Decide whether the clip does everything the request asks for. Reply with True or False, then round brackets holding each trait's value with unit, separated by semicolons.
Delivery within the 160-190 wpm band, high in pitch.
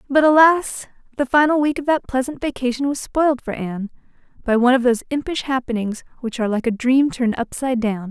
False (200 wpm; 260 Hz)